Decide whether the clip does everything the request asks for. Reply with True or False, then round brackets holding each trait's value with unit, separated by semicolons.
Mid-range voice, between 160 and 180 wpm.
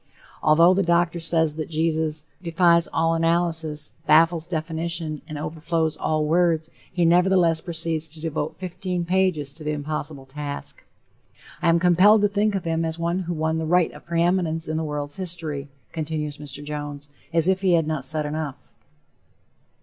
True (165 Hz; 165 wpm)